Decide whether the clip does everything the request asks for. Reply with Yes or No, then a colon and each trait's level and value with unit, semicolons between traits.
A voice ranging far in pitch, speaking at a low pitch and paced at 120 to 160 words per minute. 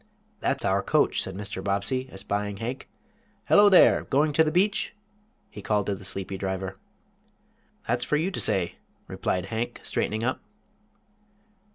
Yes: wide, 5.7 semitones; low, 105 Hz; average, 150 wpm